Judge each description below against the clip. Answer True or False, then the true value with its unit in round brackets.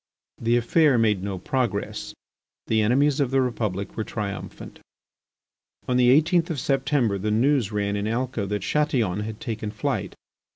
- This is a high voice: False (115 Hz)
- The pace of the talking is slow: False (155 wpm)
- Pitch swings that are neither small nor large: True (4.4 semitones)